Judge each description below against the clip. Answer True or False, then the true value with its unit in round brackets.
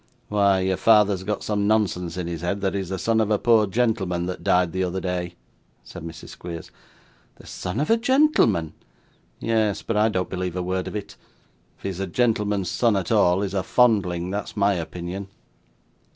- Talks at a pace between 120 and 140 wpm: False (195 wpm)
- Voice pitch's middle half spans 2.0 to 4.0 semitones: True (2.9 semitones)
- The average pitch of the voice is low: True (95 Hz)